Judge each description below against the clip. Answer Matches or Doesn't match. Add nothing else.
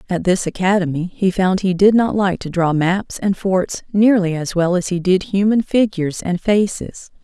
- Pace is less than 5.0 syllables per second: Matches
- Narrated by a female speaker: Matches